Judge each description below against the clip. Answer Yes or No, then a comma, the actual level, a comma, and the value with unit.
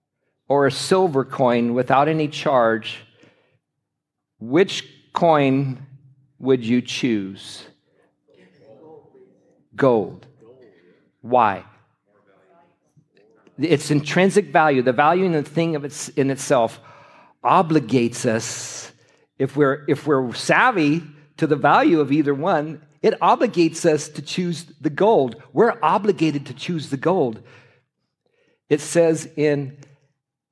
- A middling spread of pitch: Yes, average, 3.2 semitones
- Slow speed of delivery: Yes, slow, 110 wpm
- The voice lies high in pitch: No, medium, 145 Hz